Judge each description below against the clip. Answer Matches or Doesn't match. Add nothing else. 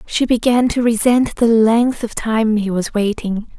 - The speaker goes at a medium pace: Matches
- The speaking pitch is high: Matches